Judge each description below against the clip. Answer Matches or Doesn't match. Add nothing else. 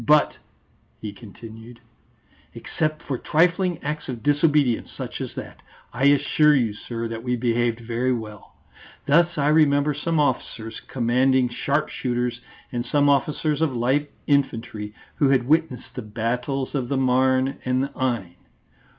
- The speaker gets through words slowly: Doesn't match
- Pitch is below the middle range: Matches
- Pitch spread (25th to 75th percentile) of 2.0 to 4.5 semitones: Matches